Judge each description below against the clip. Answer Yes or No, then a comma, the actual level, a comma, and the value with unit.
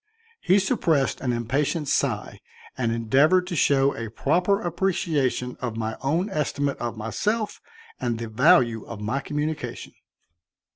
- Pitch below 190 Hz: Yes, medium, 140 Hz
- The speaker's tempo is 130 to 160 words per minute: Yes, slow, 135 wpm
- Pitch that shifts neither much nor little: No, wide, 6.4 semitones